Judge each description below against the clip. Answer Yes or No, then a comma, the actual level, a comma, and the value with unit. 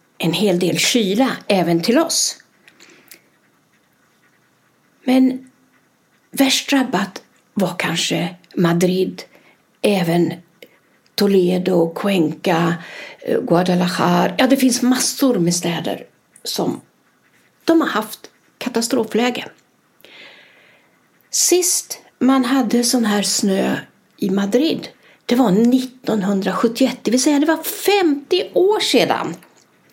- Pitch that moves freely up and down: Yes, wide, 6.4 semitones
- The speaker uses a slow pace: Yes, slow, 95 wpm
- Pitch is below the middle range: No, high, 235 Hz